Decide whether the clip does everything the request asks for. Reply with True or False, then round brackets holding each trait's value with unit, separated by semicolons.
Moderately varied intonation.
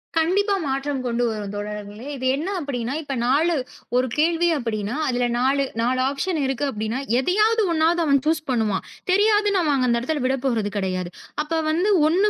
False (5.9 semitones)